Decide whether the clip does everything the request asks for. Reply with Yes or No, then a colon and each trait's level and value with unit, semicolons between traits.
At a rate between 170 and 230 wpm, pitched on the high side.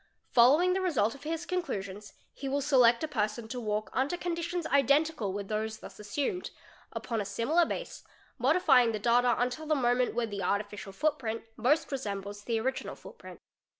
Yes: average, 185 wpm; high, 245 Hz